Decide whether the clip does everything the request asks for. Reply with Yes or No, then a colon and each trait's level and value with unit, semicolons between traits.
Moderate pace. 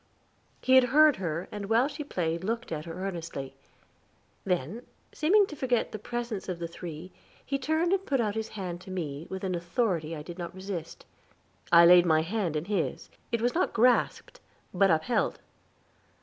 Yes: average, 180 wpm